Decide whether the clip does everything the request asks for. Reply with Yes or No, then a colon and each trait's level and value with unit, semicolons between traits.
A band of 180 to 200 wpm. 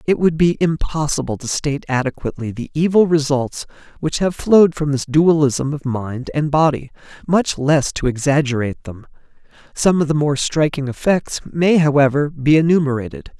No: average, 155 wpm